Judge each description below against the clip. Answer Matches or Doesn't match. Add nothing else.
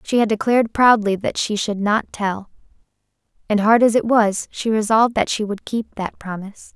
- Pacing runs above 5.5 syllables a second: Doesn't match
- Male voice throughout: Doesn't match